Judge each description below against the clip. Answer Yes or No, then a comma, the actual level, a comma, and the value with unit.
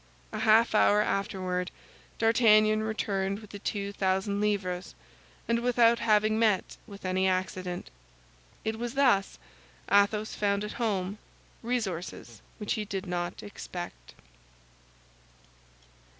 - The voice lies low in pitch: No, high, 205 Hz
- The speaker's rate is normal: No, slow, 115 wpm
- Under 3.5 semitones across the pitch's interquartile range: Yes, narrow, 2.6 semitones